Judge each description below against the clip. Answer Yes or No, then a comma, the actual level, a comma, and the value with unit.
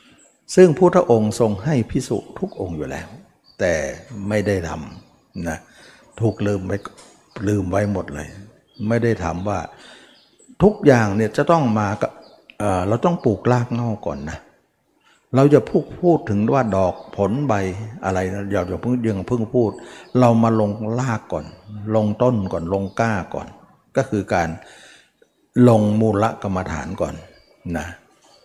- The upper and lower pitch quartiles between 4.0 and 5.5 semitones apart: No, average, 3.3 semitones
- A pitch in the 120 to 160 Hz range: No, low, 110 Hz